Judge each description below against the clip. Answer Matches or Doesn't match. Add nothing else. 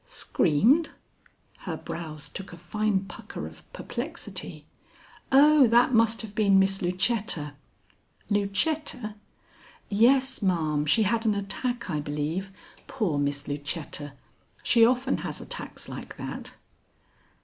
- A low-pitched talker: Doesn't match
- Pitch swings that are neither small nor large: Doesn't match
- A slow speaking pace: Matches